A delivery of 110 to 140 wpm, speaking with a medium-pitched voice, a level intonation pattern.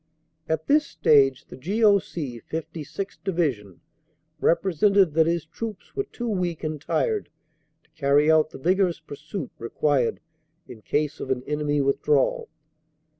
No: slow, 135 wpm; medium, 155 Hz; average, 4.8 semitones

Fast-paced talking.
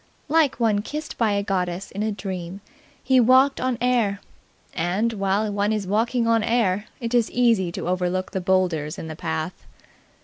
No: average, 175 wpm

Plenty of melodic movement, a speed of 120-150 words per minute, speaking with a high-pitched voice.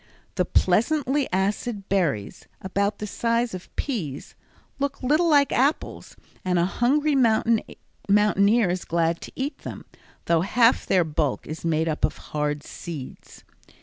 Yes: wide, 6.3 semitones; average, 140 wpm; high, 200 Hz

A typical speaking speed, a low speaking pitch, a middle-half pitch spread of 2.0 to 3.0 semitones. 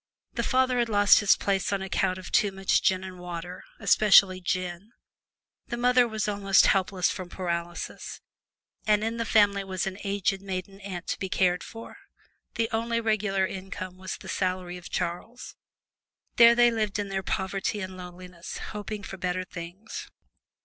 No: average, 165 wpm; high, 195 Hz; narrow, 2.5 semitones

